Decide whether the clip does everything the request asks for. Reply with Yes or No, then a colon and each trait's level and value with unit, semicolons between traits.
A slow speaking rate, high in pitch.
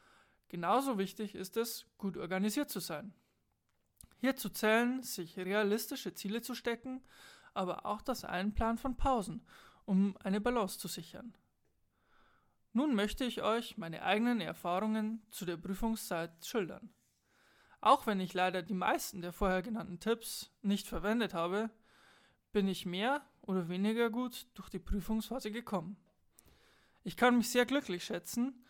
No: average, 140 wpm; high, 215 Hz